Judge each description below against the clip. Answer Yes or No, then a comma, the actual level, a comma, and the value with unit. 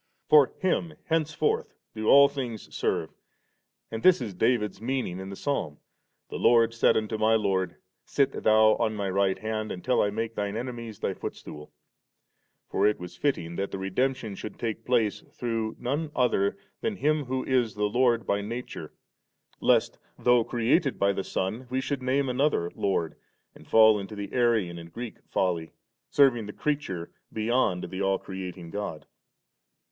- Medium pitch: No, low, 110 Hz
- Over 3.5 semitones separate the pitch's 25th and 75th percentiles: Yes, average, 4.5 semitones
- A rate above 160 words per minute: Yes, average, 170 wpm